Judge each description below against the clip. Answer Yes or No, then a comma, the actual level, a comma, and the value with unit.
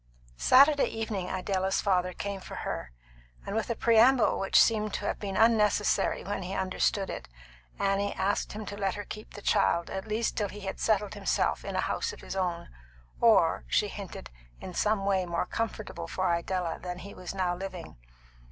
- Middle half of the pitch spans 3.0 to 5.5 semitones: No, narrow, 2.5 semitones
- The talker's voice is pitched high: Yes, high, 195 Hz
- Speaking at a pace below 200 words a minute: Yes, average, 190 wpm